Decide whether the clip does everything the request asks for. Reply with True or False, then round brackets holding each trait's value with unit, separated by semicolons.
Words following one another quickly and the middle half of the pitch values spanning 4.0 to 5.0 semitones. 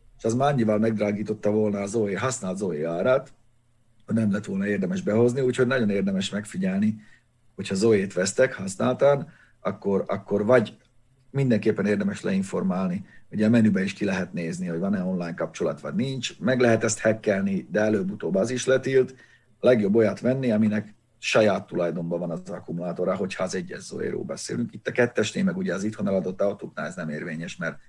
True (175 wpm; 4.3 semitones)